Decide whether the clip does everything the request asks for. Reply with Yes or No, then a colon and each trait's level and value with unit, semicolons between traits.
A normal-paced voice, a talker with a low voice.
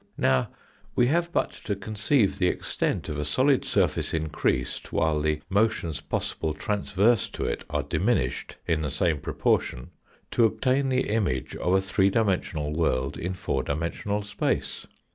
Yes: average, 155 wpm; very low, 95 Hz